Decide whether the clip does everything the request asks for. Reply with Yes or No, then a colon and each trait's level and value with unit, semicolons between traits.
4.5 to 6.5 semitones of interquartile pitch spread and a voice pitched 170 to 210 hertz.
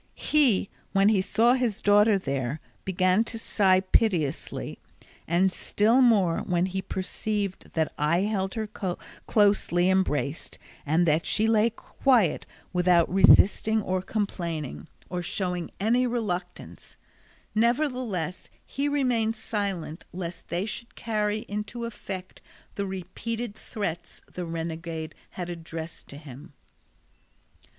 No: average, 4.1 semitones; high, 190 Hz